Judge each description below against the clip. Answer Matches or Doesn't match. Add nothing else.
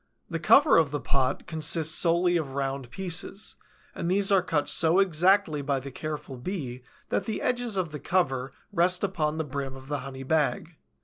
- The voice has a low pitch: Doesn't match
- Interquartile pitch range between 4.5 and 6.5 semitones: Matches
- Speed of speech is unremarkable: Matches